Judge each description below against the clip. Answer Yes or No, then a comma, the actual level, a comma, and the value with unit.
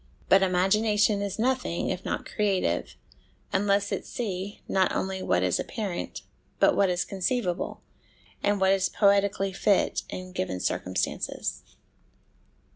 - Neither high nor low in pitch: No, high, 195 Hz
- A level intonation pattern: Yes, narrow, 1.9 semitones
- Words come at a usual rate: No, slow, 125 wpm